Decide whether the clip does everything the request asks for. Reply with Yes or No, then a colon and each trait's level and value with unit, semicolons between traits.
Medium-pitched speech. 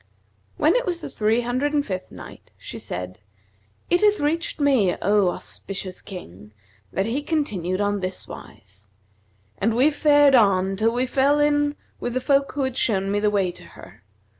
No: high, 230 Hz